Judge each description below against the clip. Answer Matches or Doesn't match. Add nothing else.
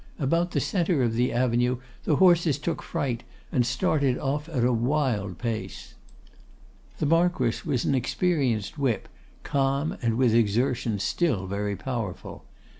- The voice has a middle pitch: Doesn't match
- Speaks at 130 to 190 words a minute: Matches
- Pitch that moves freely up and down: Doesn't match